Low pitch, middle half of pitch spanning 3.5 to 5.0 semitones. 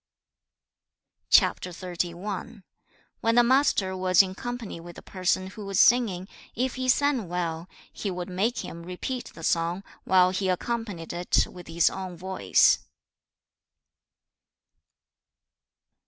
No: medium, 185 Hz; average, 4.2 semitones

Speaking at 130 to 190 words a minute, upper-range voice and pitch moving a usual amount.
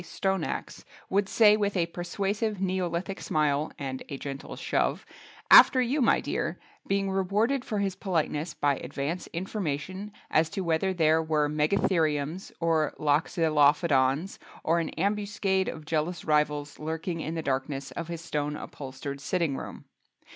No: average, 140 wpm; medium, 165 Hz; average, 4.4 semitones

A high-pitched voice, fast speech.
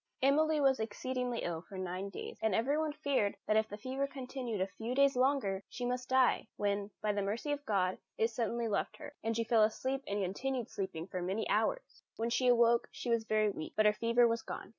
Yes: high, 230 Hz; fast, 220 wpm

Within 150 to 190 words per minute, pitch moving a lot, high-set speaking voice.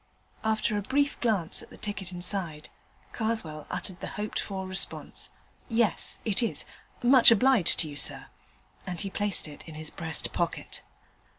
No: average, 160 wpm; average, 4.8 semitones; high, 200 Hz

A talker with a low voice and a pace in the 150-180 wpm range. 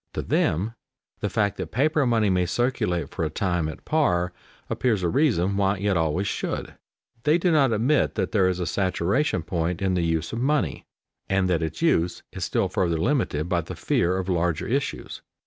No: very low, 95 Hz; average, 195 wpm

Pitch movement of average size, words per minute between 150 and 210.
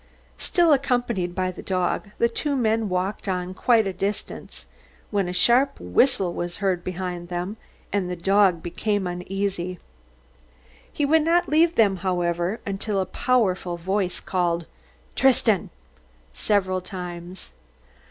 No: average, 3.8 semitones; slow, 135 wpm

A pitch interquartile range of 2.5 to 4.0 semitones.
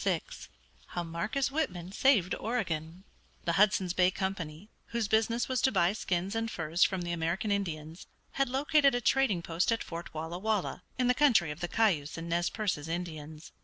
No: average, 5.2 semitones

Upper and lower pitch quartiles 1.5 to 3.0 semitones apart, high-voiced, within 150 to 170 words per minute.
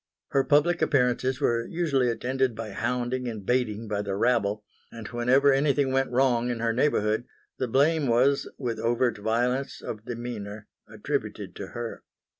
No: average, 2.7 semitones; low, 120 Hz; average, 155 wpm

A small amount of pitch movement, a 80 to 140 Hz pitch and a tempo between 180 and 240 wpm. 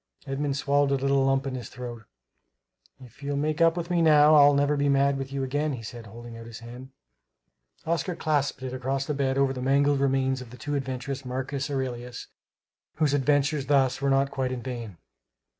Yes: narrow, 1.9 semitones; low, 135 Hz; average, 200 wpm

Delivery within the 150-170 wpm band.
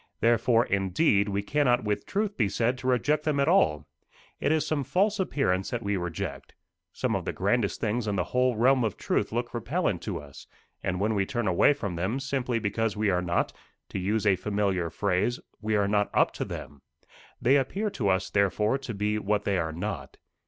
No: average, 200 wpm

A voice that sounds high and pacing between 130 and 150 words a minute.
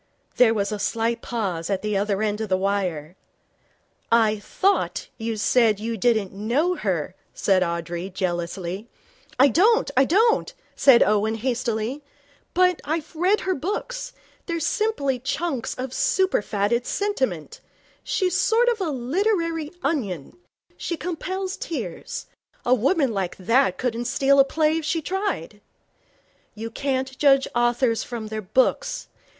Yes: high, 245 Hz; average, 140 wpm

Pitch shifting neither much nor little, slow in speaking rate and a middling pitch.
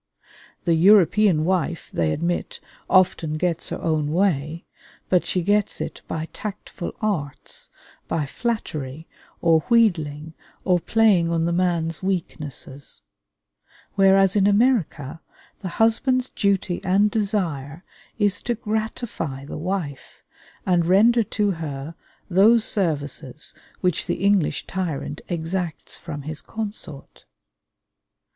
Yes: average, 4.5 semitones; slow, 115 wpm; medium, 175 Hz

